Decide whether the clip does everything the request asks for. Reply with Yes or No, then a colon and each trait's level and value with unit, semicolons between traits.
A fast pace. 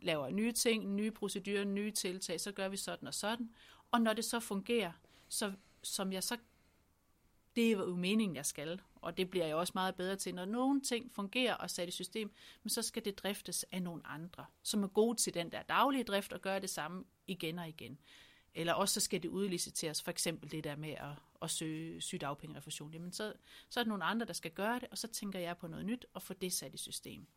Yes: fast, 230 wpm